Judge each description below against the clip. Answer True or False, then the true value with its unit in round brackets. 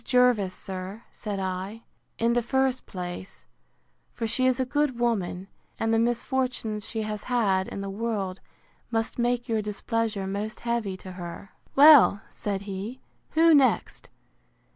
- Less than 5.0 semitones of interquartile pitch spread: True (3.8 semitones)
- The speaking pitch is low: False (220 Hz)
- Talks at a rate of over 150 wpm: False (145 wpm)